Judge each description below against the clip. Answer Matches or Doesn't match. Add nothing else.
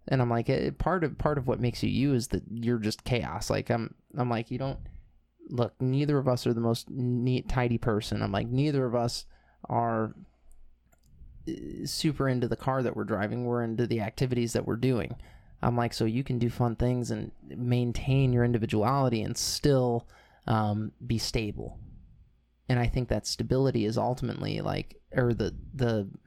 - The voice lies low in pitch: Matches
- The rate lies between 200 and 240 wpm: Doesn't match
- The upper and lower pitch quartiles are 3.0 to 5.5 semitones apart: Doesn't match